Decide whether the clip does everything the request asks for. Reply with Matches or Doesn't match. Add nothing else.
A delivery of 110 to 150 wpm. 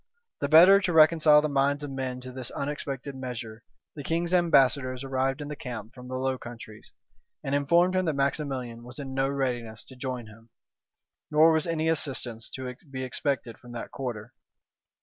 Doesn't match